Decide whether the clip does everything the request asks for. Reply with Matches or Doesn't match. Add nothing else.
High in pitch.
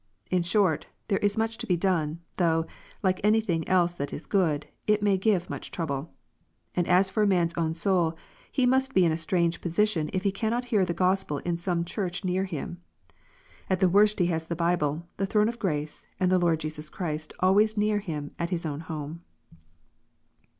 Doesn't match